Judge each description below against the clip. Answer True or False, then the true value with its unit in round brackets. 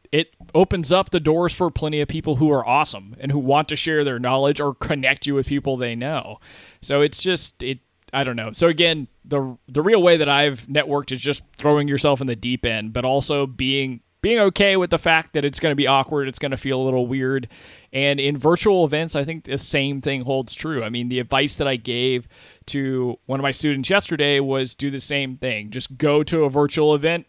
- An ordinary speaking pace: False (235 wpm)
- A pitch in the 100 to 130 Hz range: False (140 Hz)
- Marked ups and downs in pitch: False (2.6 semitones)